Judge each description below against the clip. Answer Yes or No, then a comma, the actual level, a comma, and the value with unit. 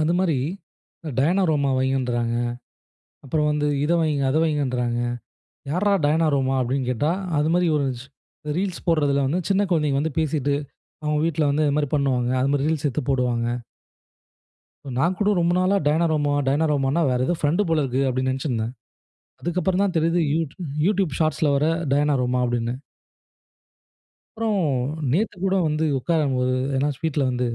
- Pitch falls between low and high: Yes, medium, 150 Hz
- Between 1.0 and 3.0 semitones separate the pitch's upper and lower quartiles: No, average, 3.6 semitones